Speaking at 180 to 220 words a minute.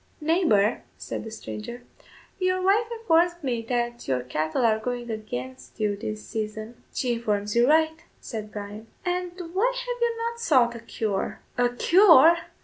No: average, 155 wpm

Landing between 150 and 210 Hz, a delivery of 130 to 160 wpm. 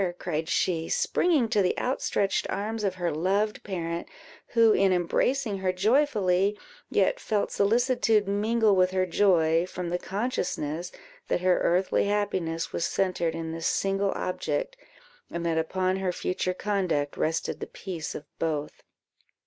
Yes: medium, 185 Hz; average, 145 wpm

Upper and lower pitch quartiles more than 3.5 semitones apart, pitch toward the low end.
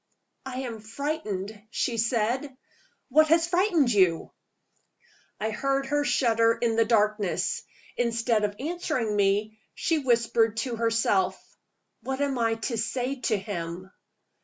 No: average, 3.9 semitones; high, 230 Hz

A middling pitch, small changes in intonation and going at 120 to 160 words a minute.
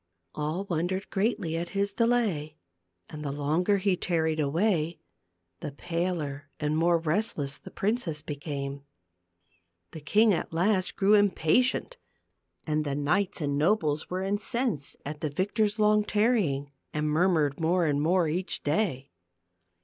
No: medium, 165 Hz; average, 5.1 semitones; average, 140 wpm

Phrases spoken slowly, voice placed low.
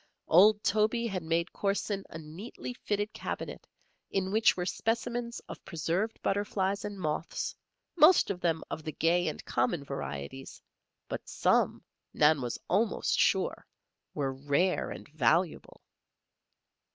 No: slow, 130 wpm; medium, 180 Hz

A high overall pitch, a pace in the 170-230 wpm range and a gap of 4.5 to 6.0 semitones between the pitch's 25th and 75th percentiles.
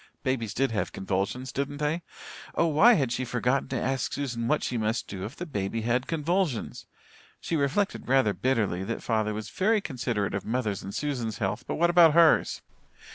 No: low, 125 Hz; average, 185 wpm; average, 5.3 semitones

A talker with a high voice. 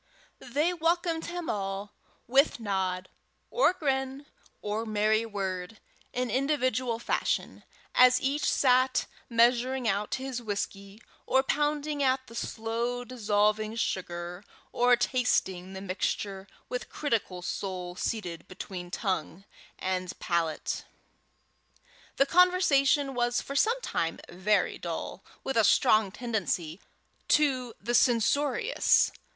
Yes: high, 230 Hz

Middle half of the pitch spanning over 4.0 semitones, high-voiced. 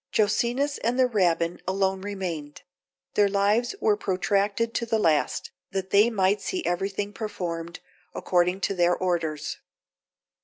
No: average, 3.2 semitones; high, 195 Hz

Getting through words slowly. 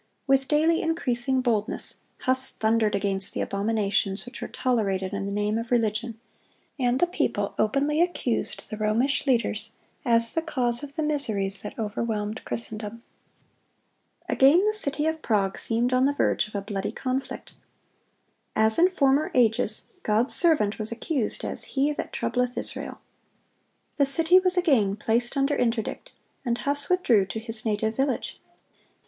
No: average, 155 wpm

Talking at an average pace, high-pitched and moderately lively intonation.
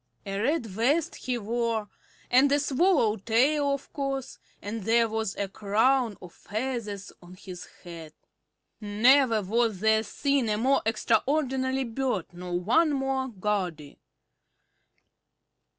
No: slow, 125 wpm; high, 230 Hz; average, 4.6 semitones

